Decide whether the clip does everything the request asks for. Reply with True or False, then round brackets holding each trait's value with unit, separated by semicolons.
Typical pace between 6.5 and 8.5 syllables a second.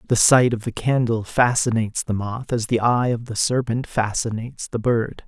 False (5.0 syllables/s)